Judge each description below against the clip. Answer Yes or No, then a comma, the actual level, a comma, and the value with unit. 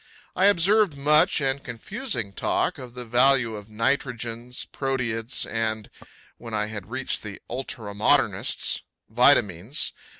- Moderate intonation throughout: Yes, average, 3.7 semitones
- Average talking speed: No, slow, 125 wpm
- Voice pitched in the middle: No, low, 120 Hz